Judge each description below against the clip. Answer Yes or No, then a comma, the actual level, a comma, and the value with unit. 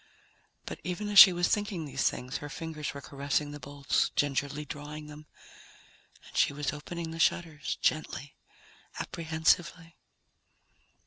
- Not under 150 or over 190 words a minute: No, slow, 135 wpm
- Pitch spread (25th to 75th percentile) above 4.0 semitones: No, narrow, 2.5 semitones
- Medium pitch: Yes, medium, 150 Hz